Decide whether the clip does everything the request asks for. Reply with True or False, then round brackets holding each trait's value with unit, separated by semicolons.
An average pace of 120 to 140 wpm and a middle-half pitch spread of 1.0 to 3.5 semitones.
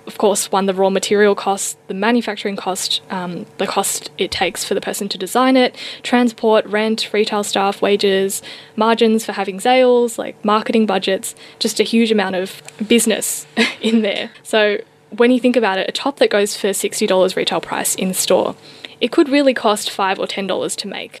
False (185 wpm; 3.2 semitones)